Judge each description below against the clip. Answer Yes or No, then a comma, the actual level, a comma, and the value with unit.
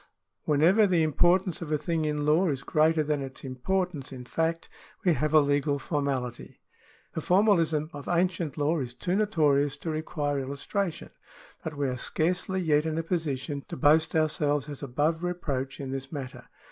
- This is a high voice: No, medium, 155 Hz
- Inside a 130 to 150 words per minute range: No, average, 170 wpm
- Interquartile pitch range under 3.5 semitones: Yes, average, 2.9 semitones